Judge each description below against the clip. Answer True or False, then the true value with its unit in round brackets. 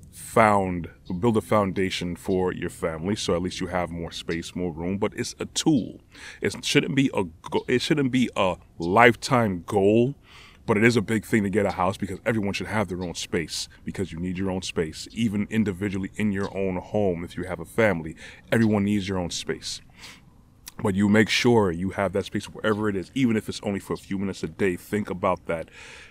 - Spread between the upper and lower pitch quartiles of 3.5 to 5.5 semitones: False (3.1 semitones)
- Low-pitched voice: True (100 Hz)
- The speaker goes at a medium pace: False (215 wpm)